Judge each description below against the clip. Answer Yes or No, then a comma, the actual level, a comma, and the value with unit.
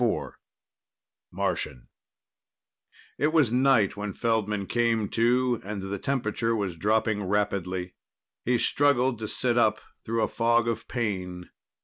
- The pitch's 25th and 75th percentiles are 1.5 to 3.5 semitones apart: Yes, average, 3.0 semitones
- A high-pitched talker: No, low, 110 Hz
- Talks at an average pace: No, slow, 125 wpm